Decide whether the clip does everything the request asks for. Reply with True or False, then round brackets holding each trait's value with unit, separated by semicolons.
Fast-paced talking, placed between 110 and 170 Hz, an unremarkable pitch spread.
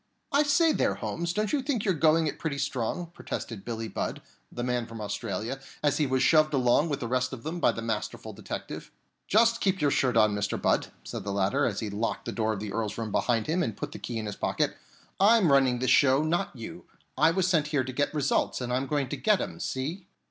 False (240 wpm; 135 Hz; 6.3 semitones)